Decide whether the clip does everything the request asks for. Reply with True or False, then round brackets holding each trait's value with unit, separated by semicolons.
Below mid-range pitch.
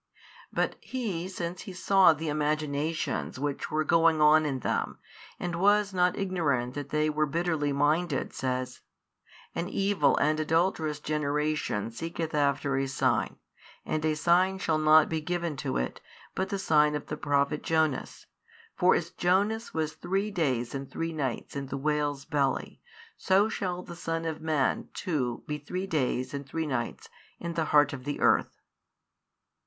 False (155 Hz)